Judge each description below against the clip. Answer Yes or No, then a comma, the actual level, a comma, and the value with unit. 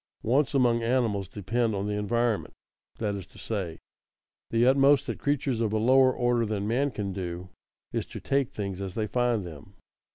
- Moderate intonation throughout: Yes, average, 3.7 semitones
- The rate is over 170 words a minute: Yes, average, 185 wpm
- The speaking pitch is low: Yes, low, 115 Hz